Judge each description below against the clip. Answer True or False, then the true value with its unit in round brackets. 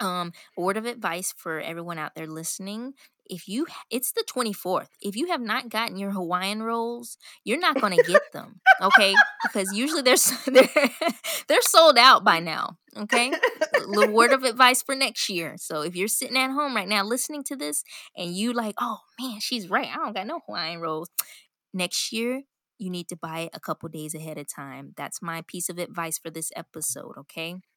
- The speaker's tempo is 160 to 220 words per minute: True (205 wpm)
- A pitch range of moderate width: False (7.0 semitones)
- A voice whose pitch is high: True (210 Hz)